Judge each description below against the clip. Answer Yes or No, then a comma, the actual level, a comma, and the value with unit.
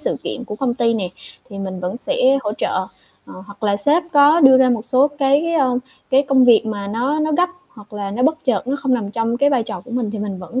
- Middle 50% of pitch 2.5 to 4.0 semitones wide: No, average, 4.7 semitones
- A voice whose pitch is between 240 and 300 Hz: Yes, high, 245 Hz